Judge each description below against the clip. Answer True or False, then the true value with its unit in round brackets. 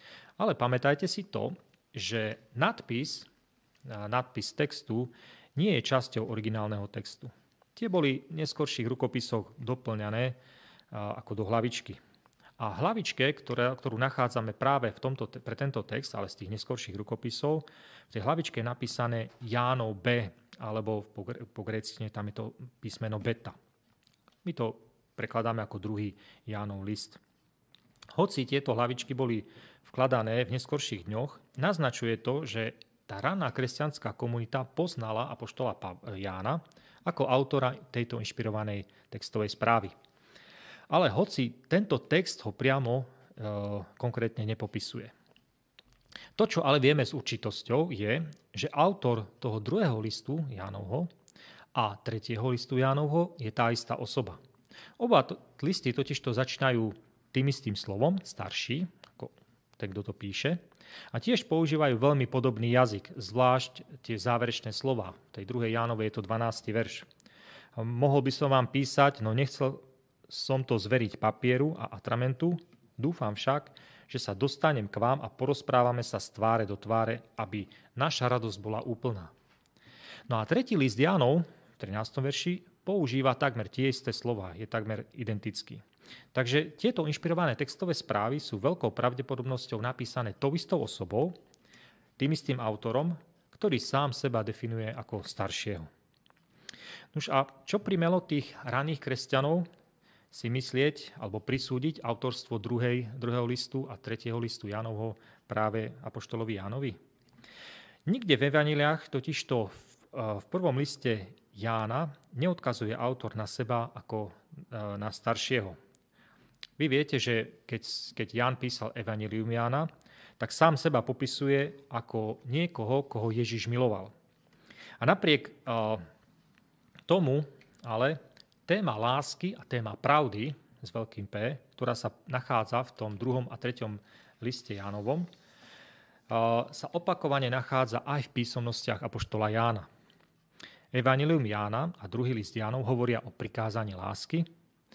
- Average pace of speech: True (130 wpm)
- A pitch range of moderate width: True (3.9 semitones)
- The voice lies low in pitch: True (125 Hz)